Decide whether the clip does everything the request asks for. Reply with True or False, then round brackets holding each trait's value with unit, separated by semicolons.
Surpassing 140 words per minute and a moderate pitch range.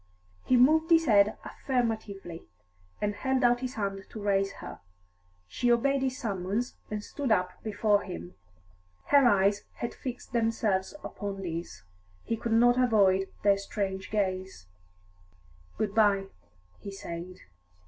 False (135 wpm; 3.8 semitones)